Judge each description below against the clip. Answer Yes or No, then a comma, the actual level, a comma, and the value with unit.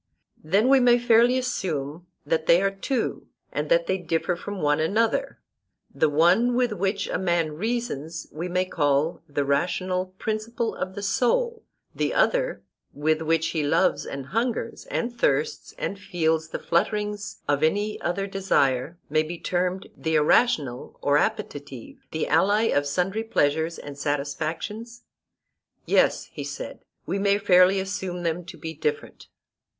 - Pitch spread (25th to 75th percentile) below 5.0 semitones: No, wide, 5.5 semitones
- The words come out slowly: No, average, 150 wpm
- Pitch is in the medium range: Yes, medium, 180 Hz